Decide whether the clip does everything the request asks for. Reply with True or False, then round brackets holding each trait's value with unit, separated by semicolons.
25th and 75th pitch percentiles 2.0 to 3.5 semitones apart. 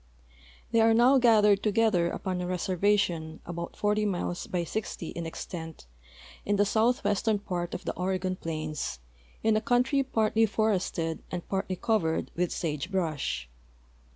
False (4.1 semitones)